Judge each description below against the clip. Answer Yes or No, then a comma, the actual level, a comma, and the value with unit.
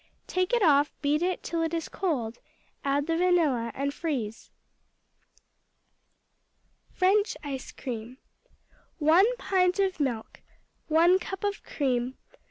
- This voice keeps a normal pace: No, slow, 120 wpm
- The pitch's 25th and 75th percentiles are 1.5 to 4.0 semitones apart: No, wide, 5.4 semitones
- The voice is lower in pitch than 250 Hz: No, very high, 315 Hz